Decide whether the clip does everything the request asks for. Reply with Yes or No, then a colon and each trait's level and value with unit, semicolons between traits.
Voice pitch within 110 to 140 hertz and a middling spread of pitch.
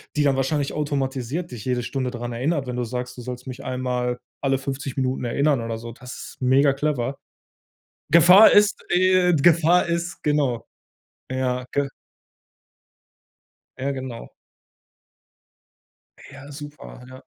Yes: low, 135 Hz; average, 3.0 semitones